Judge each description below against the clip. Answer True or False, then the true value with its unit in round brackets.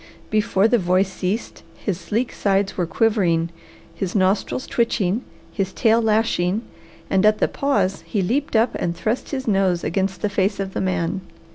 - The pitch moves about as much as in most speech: True (3.0 semitones)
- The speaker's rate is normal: True (165 wpm)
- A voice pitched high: True (195 Hz)